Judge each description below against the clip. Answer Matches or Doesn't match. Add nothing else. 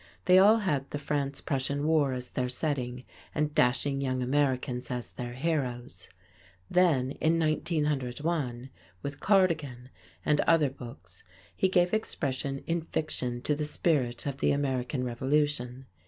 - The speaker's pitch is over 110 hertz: Matches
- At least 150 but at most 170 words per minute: Doesn't match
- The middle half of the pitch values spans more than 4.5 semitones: Doesn't match